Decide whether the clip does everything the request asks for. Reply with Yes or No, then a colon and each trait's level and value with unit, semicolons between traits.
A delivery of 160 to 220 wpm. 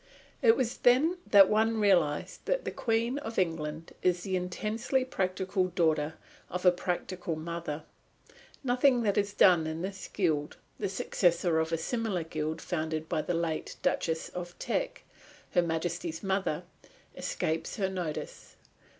No: average, 145 wpm